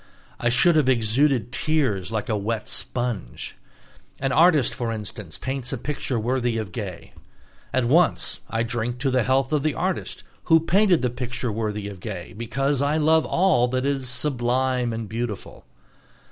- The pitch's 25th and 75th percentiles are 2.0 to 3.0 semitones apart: No, average, 3.7 semitones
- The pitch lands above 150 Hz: No, low, 125 Hz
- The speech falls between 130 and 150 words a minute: No, average, 165 wpm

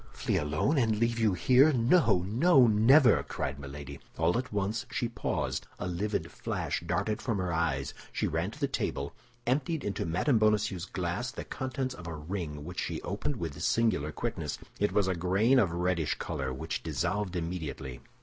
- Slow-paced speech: No, average, 180 wpm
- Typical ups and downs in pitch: No, wide, 5.9 semitones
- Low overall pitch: Yes, very low, 95 Hz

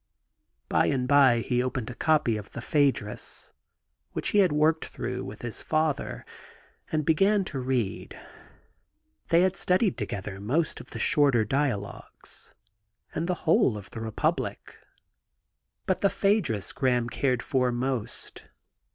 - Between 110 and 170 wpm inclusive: Yes, average, 140 wpm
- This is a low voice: Yes, low, 130 Hz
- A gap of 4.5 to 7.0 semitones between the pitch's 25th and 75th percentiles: Yes, average, 5.3 semitones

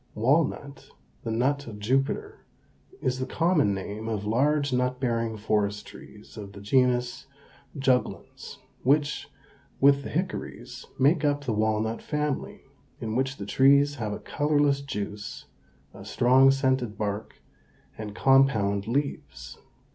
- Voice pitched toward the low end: Yes, low, 125 Hz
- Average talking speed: No, slow, 130 wpm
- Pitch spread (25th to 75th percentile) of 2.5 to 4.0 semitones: No, average, 4.6 semitones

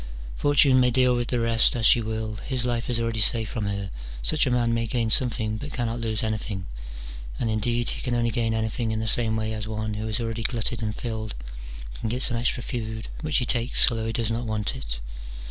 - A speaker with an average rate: No, fast, 230 wpm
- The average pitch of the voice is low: Yes, low, 115 Hz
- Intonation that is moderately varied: No, narrow, 1.7 semitones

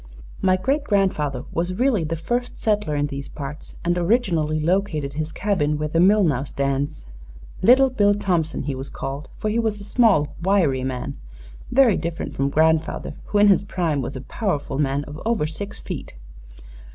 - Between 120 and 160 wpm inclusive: No, average, 175 wpm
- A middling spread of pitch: No, wide, 5.8 semitones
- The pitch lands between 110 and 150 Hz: No, medium, 165 Hz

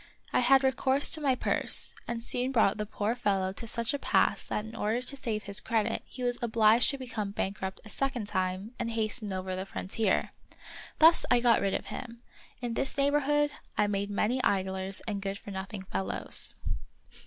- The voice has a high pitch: Yes, high, 220 Hz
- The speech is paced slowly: No, average, 190 wpm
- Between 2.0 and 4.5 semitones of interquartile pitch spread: Yes, average, 4.0 semitones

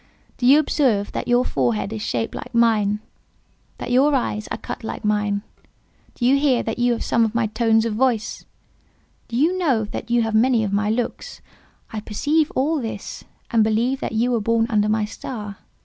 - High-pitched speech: Yes, high, 230 Hz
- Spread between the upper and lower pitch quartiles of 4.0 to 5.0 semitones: No, average, 2.9 semitones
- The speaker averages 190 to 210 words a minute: Yes, average, 195 wpm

